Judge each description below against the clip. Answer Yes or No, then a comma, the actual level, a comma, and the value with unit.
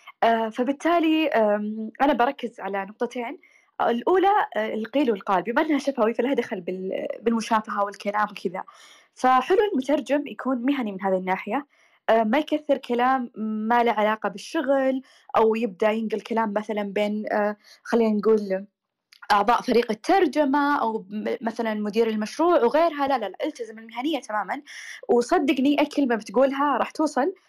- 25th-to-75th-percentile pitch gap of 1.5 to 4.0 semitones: No, average, 5.0 semitones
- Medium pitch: No, high, 240 Hz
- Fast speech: No, average, 120 wpm